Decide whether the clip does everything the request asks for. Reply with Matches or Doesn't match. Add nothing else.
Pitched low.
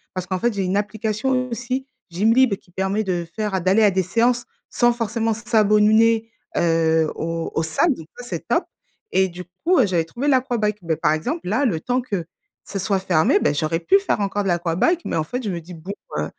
Doesn't match